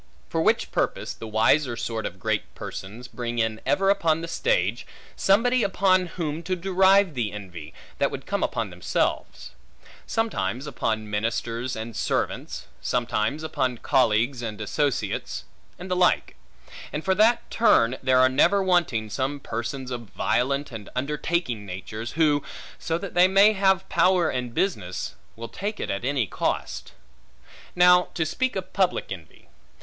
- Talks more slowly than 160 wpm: Yes, average, 150 wpm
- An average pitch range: No, wide, 8.0 semitones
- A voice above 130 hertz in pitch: Yes, medium, 140 Hz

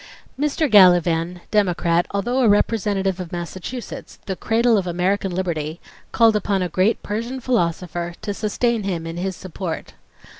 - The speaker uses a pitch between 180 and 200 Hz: Yes, high, 190 Hz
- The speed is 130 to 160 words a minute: Yes, average, 145 wpm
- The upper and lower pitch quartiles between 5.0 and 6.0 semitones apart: No, average, 3.9 semitones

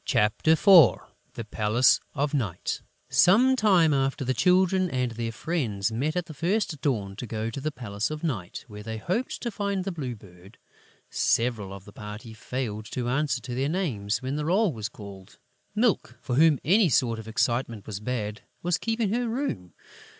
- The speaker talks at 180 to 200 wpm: Yes, average, 185 wpm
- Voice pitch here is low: Yes, low, 130 Hz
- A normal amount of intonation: No, wide, 7.9 semitones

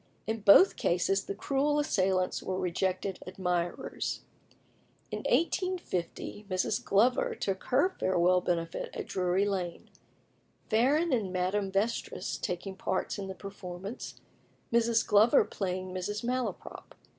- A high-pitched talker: Yes, high, 195 Hz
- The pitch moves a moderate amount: Yes, average, 3.9 semitones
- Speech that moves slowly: Yes, slow, 120 wpm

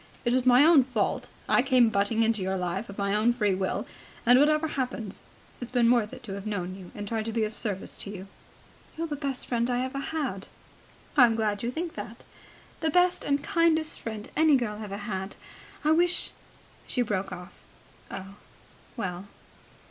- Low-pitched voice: No, high, 230 Hz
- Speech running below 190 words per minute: No, average, 195 wpm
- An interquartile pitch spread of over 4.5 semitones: Yes, average, 5.1 semitones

